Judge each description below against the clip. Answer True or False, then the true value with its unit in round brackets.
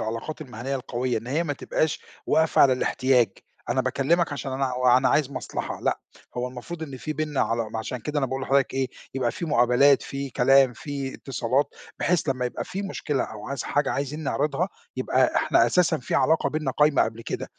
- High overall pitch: False (135 Hz)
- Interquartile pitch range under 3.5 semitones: True (2.8 semitones)